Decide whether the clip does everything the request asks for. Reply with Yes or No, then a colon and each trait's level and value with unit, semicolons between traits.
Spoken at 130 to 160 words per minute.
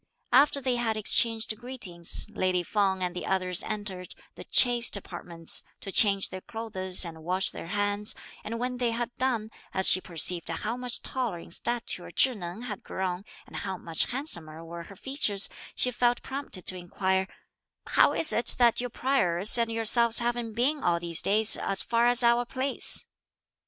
No: average, 175 wpm